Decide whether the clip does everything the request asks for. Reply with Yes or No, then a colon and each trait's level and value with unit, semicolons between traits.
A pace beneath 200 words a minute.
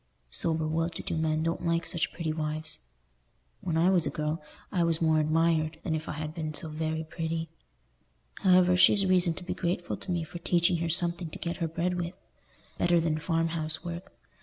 No: fast, 205 wpm